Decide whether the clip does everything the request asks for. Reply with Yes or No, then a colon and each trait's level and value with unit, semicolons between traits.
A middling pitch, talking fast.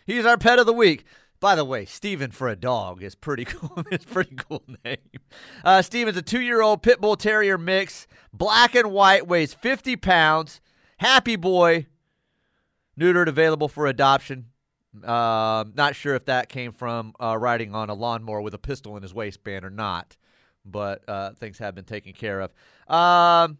No: medium, 145 Hz; average, 185 wpm